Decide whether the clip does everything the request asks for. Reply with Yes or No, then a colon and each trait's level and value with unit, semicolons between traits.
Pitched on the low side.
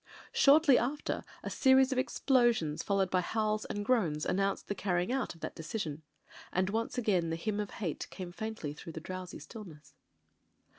No: high, 200 Hz